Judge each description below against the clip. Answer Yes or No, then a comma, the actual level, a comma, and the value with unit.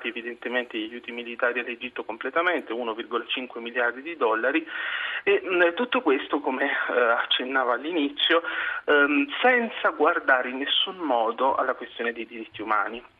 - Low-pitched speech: No, medium, 165 Hz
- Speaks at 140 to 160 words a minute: No, average, 120 wpm